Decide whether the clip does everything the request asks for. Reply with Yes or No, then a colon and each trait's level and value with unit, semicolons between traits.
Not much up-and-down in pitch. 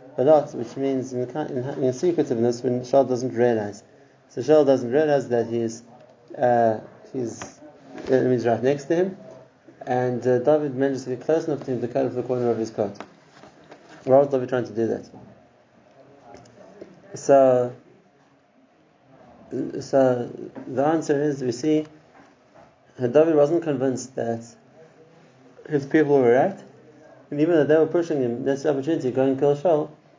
No: average, 3.2 semitones